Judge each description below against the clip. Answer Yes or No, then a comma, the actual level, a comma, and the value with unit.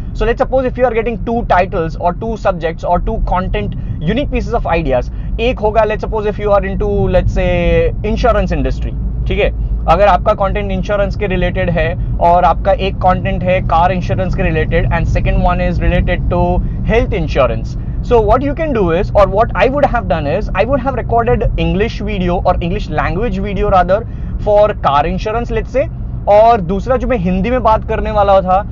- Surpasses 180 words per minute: Yes, fast, 205 wpm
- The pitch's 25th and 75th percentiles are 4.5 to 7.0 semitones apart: No, average, 3.8 semitones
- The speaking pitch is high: Yes, high, 195 Hz